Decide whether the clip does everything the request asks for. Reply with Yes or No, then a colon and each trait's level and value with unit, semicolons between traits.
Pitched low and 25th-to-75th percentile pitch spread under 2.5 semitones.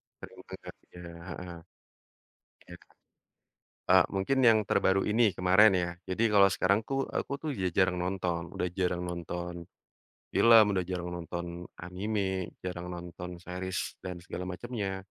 Yes: very low, 90 Hz; narrow, 2.0 semitones